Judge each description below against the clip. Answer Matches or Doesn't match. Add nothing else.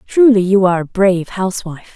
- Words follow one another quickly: Doesn't match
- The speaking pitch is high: Matches